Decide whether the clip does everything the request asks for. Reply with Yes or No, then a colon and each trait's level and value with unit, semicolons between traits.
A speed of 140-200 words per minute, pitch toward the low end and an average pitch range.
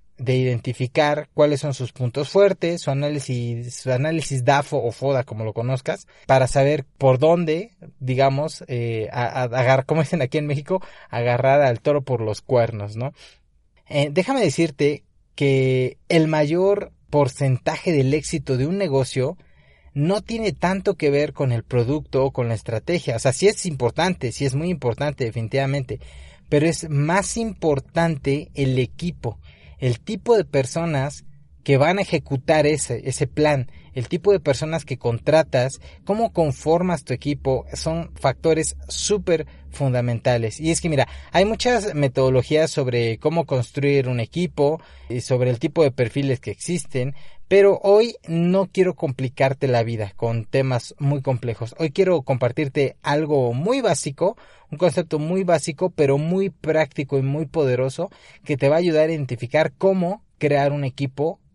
No: average, 155 wpm; medium, 145 Hz; average, 4.4 semitones